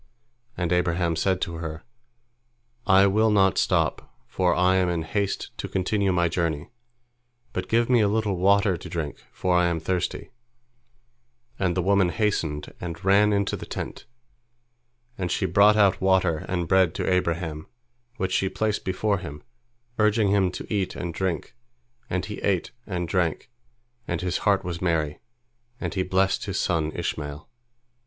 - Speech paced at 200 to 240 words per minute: No, average, 160 wpm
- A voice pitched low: Yes, very low, 95 Hz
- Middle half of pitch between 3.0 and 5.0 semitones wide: No, narrow, 2.6 semitones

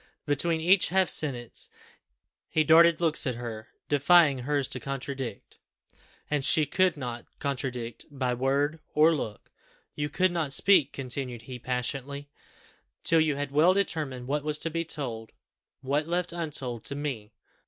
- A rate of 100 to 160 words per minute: Yes, average, 150 wpm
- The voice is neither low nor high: Yes, medium, 145 Hz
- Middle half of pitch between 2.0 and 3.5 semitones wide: No, average, 4.0 semitones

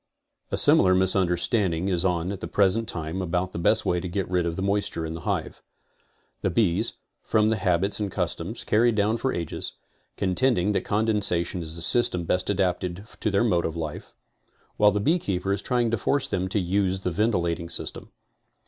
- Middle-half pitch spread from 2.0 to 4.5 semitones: Yes, average, 3.2 semitones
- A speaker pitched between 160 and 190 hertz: No, very low, 95 Hz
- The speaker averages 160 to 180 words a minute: No, average, 190 wpm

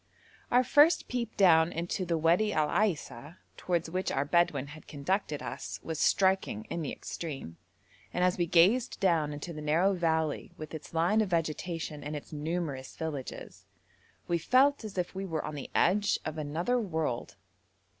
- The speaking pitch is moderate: Yes, medium, 165 Hz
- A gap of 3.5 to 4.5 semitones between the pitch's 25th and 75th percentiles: Yes, average, 3.8 semitones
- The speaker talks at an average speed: Yes, average, 170 wpm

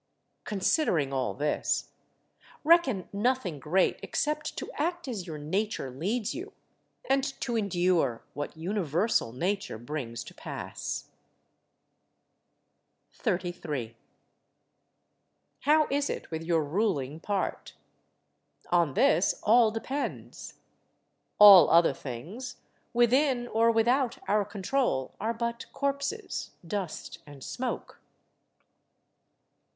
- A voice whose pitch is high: Yes, high, 200 Hz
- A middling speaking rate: No, slow, 100 wpm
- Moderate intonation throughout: No, wide, 7.6 semitones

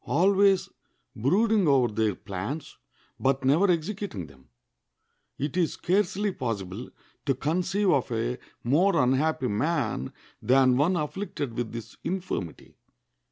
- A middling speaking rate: No, slow, 115 wpm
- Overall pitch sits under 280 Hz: Yes, medium, 140 Hz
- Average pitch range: No, wide, 7.5 semitones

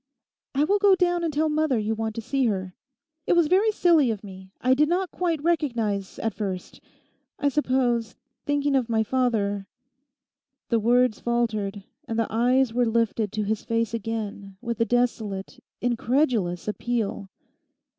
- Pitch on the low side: No, high, 235 Hz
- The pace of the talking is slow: No, average, 155 wpm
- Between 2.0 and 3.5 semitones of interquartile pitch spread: No, average, 4.9 semitones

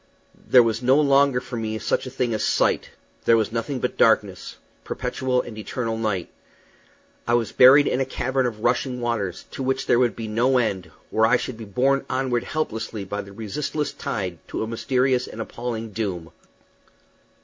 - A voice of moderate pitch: No, low, 120 Hz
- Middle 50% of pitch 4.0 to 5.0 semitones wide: No, average, 2.9 semitones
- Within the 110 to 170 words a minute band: No, average, 185 wpm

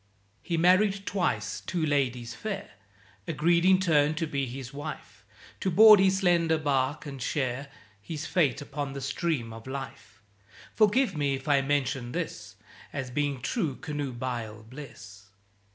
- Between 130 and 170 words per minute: Yes, average, 145 wpm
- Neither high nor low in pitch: Yes, medium, 145 Hz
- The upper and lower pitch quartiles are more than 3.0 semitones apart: Yes, average, 4.7 semitones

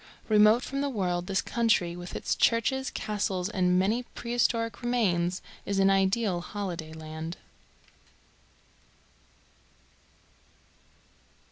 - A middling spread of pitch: Yes, average, 4.5 semitones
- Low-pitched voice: No, high, 195 Hz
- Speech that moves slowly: Yes, slow, 100 wpm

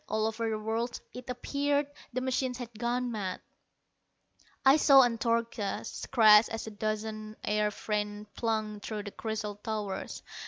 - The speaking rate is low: No, average, 145 wpm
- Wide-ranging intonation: No, narrow, 2.4 semitones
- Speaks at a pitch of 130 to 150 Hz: No, high, 220 Hz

